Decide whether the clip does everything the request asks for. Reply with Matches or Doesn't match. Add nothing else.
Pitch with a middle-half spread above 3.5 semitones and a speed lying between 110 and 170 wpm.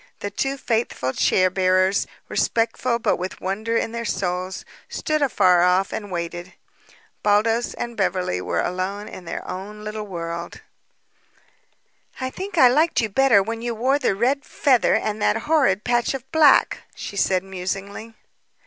Matches